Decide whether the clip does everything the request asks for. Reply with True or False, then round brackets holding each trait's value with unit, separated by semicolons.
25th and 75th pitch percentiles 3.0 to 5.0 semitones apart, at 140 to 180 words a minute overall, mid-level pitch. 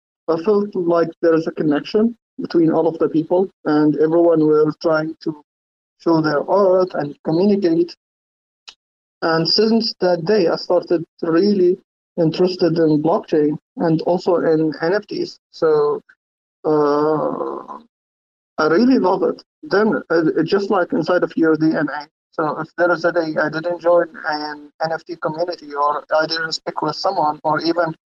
False (2.6 semitones; 150 wpm; 165 Hz)